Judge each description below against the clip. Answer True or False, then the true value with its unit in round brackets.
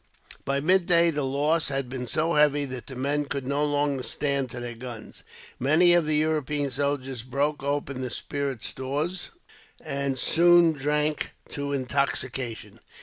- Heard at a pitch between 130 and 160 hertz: True (140 Hz)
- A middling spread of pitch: False (2.3 semitones)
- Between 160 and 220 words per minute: False (150 wpm)